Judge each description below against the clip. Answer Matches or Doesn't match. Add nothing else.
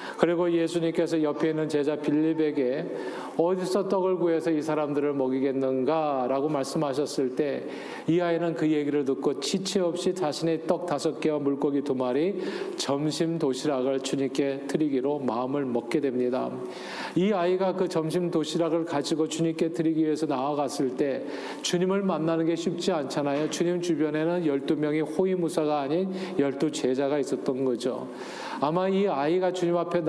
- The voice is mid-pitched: Matches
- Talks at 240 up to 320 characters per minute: Doesn't match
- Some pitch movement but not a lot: Matches